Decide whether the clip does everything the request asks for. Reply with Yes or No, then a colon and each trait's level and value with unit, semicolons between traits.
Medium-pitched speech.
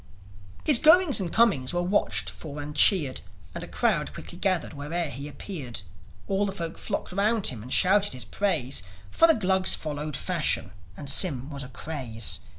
Yes: medium, 160 Hz